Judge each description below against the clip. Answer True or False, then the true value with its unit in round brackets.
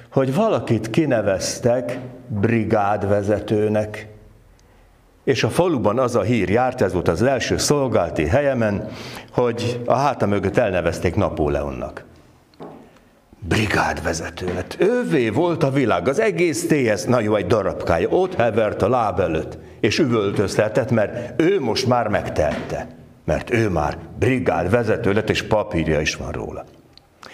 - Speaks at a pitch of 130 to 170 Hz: False (105 Hz)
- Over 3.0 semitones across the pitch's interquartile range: True (4.2 semitones)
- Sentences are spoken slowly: False (125 wpm)